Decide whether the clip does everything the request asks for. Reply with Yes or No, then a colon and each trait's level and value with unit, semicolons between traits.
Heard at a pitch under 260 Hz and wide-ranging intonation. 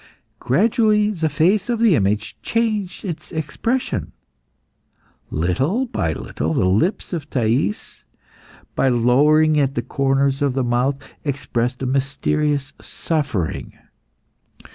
Yes: medium, 140 Hz; wide, 6.2 semitones